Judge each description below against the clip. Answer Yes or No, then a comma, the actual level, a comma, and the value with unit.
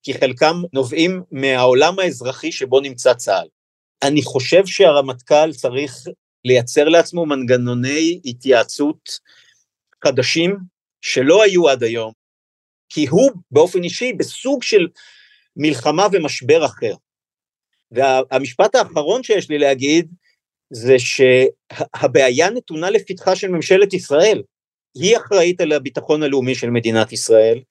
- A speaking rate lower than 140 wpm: Yes, average, 110 wpm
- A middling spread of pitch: No, wide, 5.9 semitones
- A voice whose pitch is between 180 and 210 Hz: No, medium, 150 Hz